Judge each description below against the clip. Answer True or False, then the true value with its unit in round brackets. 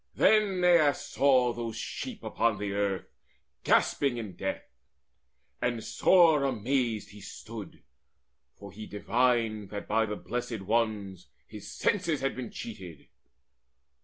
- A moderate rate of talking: False (125 wpm)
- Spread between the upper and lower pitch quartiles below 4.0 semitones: False (4.6 semitones)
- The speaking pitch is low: True (115 Hz)